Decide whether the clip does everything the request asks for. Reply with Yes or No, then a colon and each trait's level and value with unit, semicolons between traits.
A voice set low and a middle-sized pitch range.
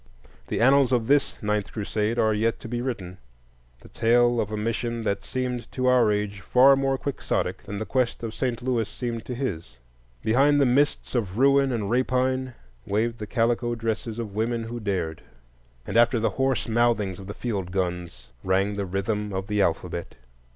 Yes: low, 115 Hz; average, 3.6 semitones